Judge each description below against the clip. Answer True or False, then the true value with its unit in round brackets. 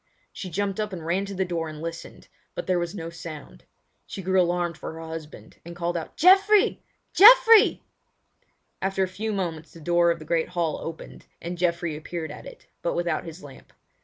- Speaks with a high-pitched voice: False (175 Hz)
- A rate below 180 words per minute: False (195 wpm)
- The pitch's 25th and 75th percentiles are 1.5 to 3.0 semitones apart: True (2.6 semitones)